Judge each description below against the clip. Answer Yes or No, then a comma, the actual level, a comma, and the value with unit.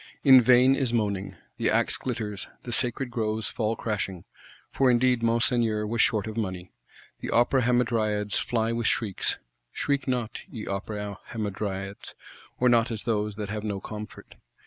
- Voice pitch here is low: Yes, low, 110 Hz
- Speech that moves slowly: No, average, 150 wpm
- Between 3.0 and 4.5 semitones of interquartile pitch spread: No, narrow, 2.5 semitones